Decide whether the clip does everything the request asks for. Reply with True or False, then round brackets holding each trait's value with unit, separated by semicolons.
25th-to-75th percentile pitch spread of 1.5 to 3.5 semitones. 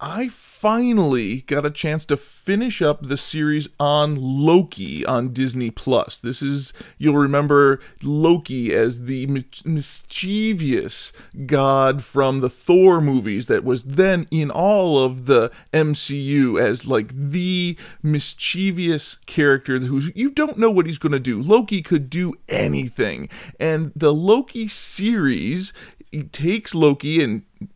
False (4.9 semitones)